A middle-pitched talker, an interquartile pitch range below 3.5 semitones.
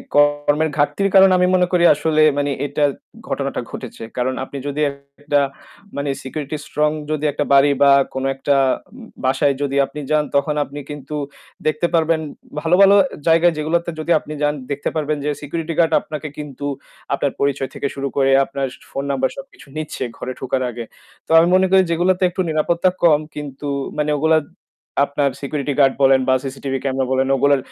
Yes: medium, 145 Hz; narrow, 2.4 semitones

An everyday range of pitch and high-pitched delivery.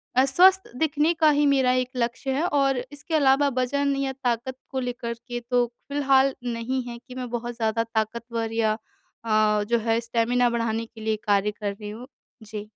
Yes: average, 3.0 semitones; high, 245 Hz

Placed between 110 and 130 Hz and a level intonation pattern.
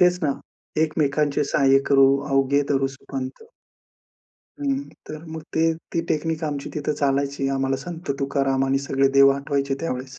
No: medium, 140 Hz; narrow, 2.0 semitones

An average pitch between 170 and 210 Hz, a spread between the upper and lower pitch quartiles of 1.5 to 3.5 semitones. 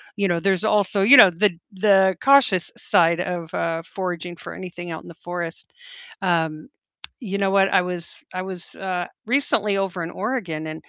Yes: medium, 185 Hz; narrow, 2.5 semitones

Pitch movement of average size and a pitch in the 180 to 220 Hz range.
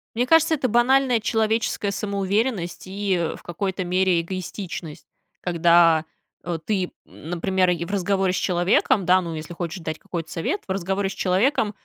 Yes: average, 3.1 semitones; medium, 185 Hz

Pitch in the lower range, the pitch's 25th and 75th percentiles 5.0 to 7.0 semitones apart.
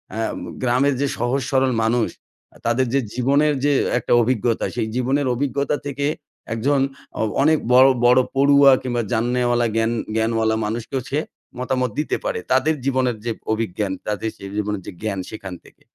No: low, 125 Hz; average, 3.4 semitones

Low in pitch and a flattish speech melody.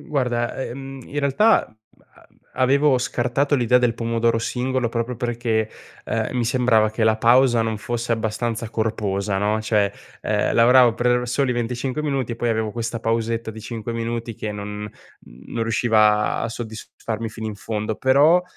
Yes: low, 115 Hz; narrow, 2.1 semitones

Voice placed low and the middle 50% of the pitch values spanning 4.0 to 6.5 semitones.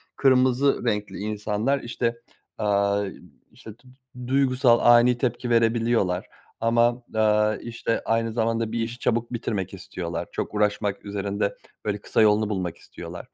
No: low, 115 Hz; narrow, 2.6 semitones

